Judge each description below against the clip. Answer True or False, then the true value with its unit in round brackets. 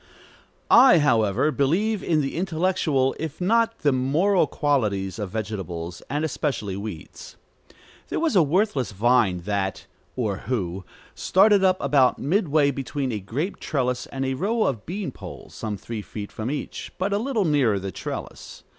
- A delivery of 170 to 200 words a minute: False (155 wpm)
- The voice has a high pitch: False (135 Hz)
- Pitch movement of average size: False (8.7 semitones)